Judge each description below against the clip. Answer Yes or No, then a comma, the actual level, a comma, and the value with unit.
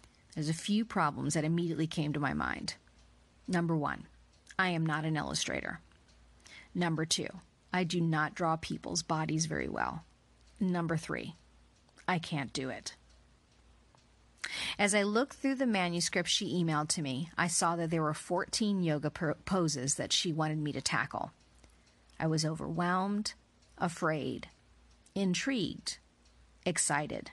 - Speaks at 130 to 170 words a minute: Yes, average, 140 wpm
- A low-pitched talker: No, medium, 160 Hz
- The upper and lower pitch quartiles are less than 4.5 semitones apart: No, average, 4.8 semitones